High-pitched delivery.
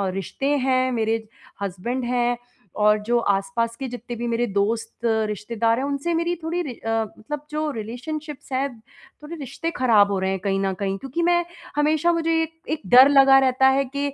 Yes: very high, 250 Hz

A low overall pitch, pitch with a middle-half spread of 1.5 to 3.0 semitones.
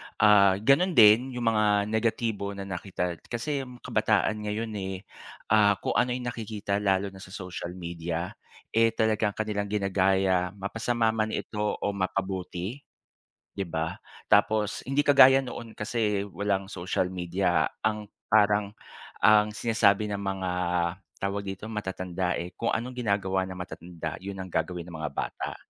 Yes: low, 100 Hz; narrow, 2.6 semitones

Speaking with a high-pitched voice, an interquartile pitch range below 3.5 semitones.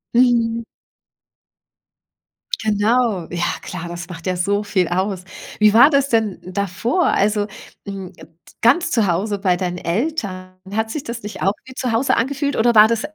No: high, 210 Hz; average, 4.2 semitones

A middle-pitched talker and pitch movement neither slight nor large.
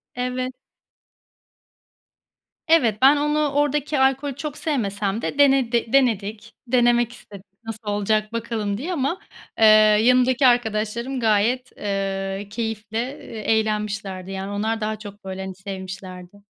No: high, 220 Hz; average, 3.9 semitones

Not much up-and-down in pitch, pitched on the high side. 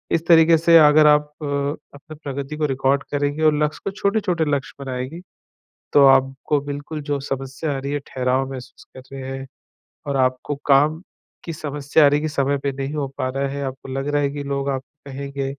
No: narrow, 1.9 semitones; medium, 140 Hz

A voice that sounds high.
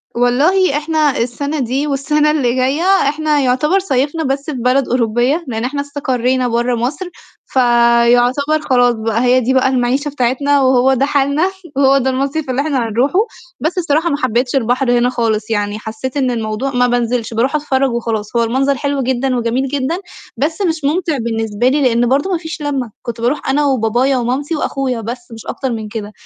Yes: very high, 260 Hz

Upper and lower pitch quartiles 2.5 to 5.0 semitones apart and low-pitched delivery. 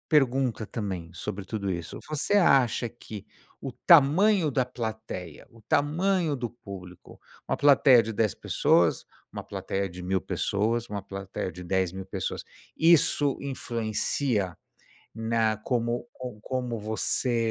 No: wide, 5.5 semitones; low, 115 Hz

